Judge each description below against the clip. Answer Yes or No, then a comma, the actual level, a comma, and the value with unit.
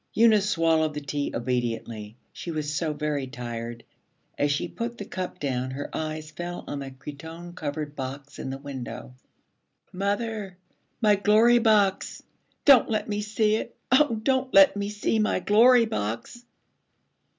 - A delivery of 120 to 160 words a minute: Yes, average, 150 wpm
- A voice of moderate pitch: Yes, medium, 165 Hz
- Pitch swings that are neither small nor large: No, wide, 7.2 semitones